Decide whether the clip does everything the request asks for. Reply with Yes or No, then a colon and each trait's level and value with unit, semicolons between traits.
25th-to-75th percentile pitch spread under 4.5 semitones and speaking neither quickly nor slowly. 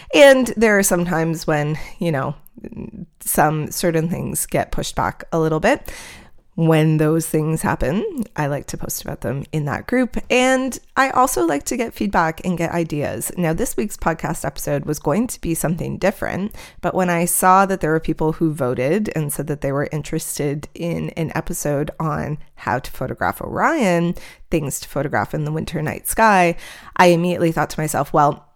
Yes: average, 3.6 semitones; average, 185 wpm